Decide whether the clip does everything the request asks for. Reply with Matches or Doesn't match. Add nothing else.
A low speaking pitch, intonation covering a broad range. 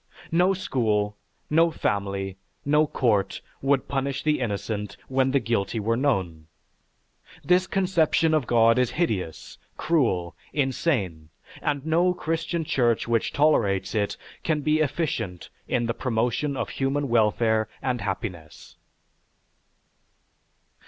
Matches